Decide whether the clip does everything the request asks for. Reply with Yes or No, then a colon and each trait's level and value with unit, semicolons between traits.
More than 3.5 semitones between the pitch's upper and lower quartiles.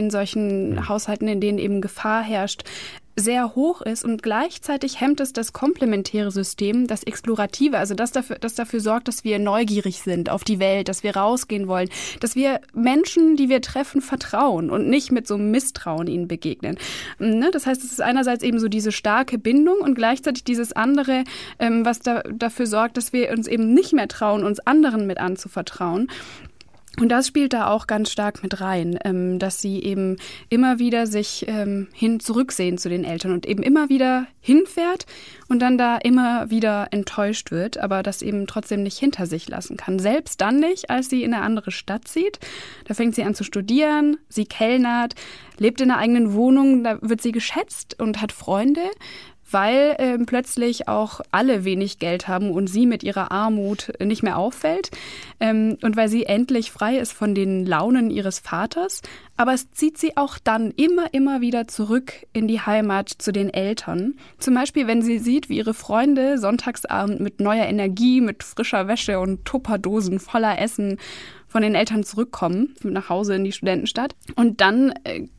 Yes: average, 3.9 semitones